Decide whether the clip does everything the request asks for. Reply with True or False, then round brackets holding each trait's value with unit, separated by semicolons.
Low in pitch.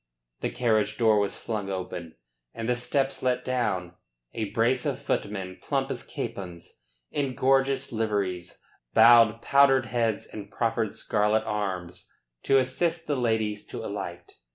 True (110 Hz)